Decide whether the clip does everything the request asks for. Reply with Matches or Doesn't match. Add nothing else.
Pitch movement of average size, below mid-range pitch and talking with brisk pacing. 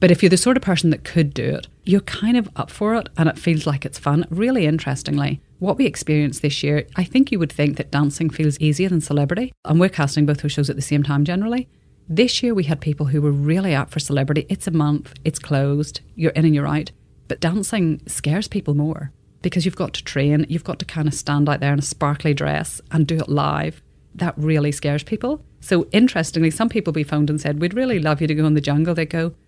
Doesn't match